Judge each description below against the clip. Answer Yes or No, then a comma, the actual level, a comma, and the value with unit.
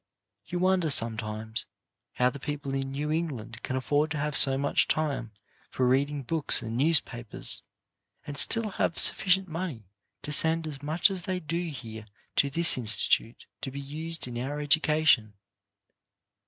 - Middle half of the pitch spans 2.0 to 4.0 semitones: No, average, 4.4 semitones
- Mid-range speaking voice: Yes, medium, 145 Hz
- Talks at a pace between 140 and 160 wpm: Yes, average, 155 wpm